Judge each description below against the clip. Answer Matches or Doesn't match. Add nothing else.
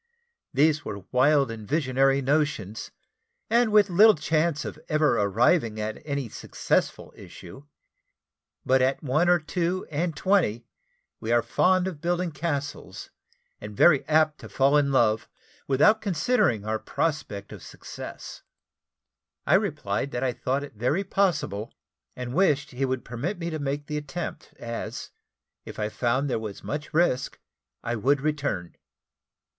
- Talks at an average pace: Matches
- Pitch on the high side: Doesn't match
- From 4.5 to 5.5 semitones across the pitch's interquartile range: Matches